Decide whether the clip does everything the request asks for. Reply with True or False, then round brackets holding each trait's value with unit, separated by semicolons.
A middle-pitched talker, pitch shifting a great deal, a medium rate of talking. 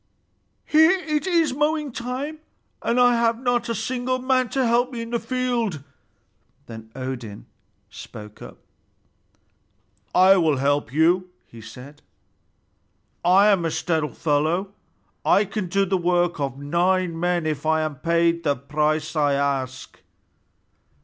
True (175 Hz; 8.6 semitones; 145 wpm)